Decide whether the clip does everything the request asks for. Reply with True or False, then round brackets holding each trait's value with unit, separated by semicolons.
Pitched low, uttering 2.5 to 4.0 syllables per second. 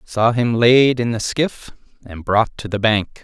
True (115 Hz; 3.9 syllables/s)